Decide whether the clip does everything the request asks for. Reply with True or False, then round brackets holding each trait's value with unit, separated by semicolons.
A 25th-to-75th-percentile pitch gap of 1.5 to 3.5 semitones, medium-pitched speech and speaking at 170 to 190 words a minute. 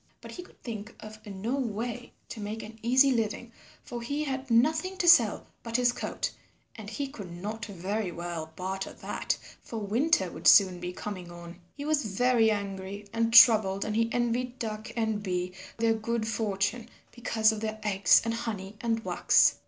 False (3.1 semitones; 220 Hz; 180 wpm)